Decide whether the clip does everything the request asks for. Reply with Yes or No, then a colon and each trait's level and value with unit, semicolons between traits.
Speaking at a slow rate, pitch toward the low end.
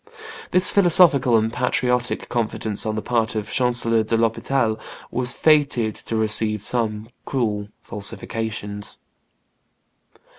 Yes: slow, 115 wpm; low, 115 Hz